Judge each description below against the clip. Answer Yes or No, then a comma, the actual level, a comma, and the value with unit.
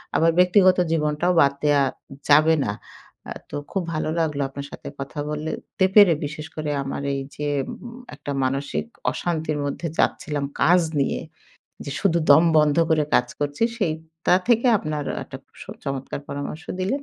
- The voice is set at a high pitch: No, medium, 155 Hz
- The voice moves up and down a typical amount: Yes, average, 3.0 semitones